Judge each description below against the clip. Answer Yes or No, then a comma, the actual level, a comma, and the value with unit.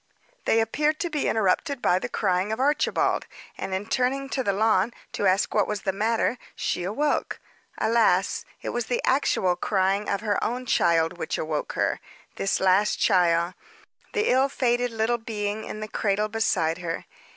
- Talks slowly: No, average, 175 wpm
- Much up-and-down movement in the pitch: No, average, 4.3 semitones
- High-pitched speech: Yes, high, 215 Hz